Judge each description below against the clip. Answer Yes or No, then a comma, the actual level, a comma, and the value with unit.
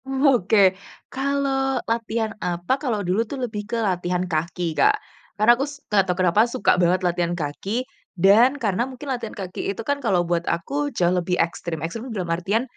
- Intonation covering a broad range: Yes, wide, 6.0 semitones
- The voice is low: No, high, 205 Hz